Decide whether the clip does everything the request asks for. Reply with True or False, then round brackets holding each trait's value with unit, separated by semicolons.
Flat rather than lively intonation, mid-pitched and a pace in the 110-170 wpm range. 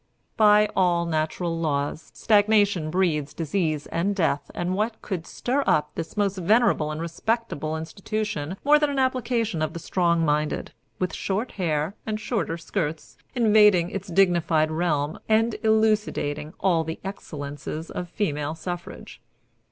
False (5.1 semitones; 175 Hz; 140 wpm)